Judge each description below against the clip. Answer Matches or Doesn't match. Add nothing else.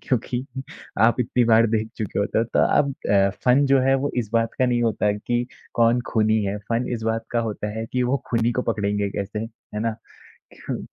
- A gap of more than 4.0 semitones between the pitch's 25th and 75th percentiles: Doesn't match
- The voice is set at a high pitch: Doesn't match